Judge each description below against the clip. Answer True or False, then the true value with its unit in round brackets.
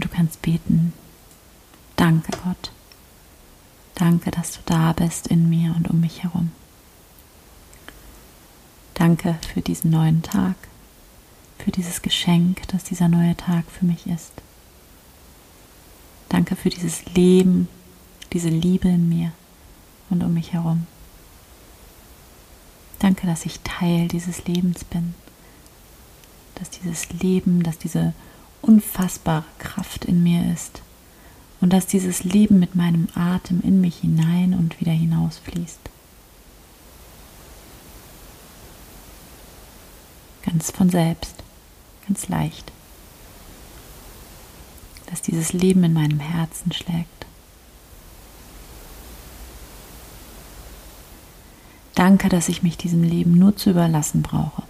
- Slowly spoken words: True (105 wpm)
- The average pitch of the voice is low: False (165 Hz)